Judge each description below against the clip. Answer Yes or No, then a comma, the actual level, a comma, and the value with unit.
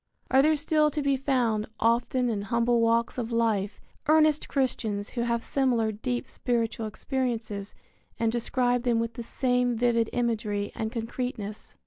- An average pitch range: No, narrow, 2.1 semitones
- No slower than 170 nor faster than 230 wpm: No, average, 150 wpm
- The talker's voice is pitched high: Yes, high, 235 Hz